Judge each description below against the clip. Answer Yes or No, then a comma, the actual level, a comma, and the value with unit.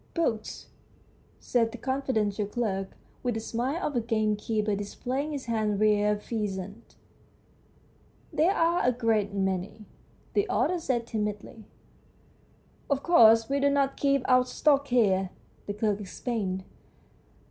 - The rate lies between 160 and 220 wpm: No, average, 145 wpm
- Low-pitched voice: No, high, 225 Hz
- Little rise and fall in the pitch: No, average, 4.2 semitones